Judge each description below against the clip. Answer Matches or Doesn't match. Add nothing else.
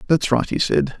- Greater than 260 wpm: Doesn't match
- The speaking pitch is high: Doesn't match